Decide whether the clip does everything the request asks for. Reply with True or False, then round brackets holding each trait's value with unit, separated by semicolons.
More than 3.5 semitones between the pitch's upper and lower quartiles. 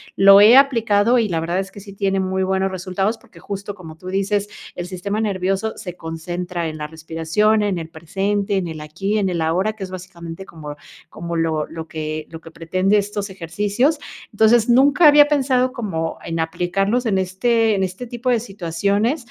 True (4.0 semitones)